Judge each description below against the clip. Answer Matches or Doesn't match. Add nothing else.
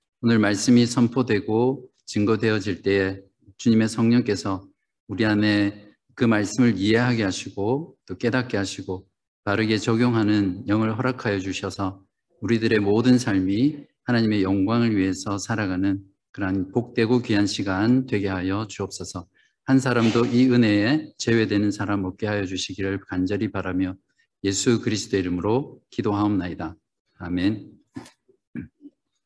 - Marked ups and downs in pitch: Doesn't match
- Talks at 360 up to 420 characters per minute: Doesn't match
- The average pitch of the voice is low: Matches